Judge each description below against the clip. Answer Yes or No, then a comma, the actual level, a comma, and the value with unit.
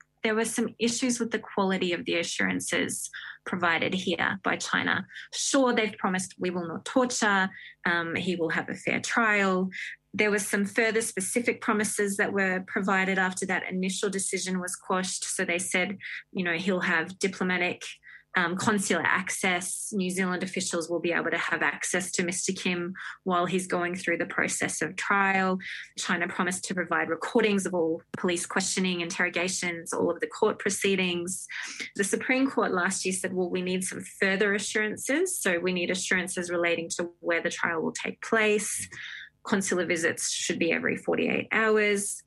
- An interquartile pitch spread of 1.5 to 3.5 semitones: Yes, average, 2.9 semitones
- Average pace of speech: Yes, average, 170 wpm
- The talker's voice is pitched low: No, high, 190 Hz